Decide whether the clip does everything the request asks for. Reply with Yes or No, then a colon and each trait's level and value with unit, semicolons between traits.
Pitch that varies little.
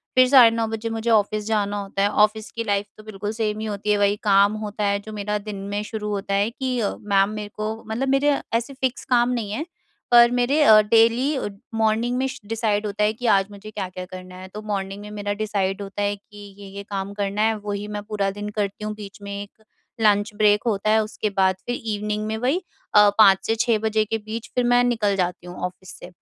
Yes: narrow, 1.8 semitones